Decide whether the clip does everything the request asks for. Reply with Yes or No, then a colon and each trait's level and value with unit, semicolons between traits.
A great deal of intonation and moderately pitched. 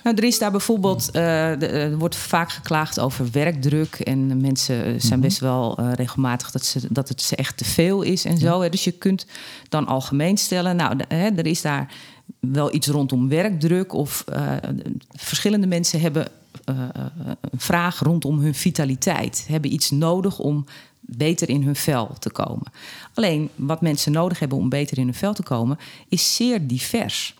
No: average, 4.6 semitones; medium, 150 Hz